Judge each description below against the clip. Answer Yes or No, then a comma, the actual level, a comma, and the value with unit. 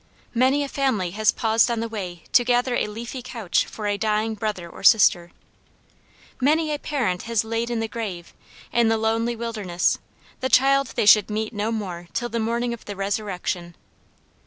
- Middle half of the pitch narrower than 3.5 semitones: Yes, average, 2.7 semitones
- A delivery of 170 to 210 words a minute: Yes, average, 180 wpm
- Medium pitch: No, high, 225 Hz